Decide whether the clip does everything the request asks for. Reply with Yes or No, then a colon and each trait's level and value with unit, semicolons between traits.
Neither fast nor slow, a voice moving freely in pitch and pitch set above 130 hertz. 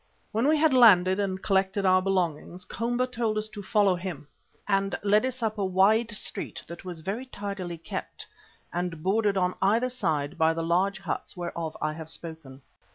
No: average, 180 wpm; average, 3.7 semitones; high, 190 Hz